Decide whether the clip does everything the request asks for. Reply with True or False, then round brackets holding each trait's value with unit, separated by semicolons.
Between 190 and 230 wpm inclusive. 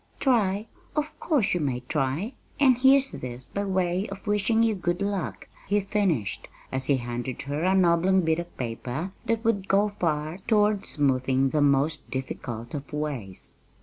False (165 wpm)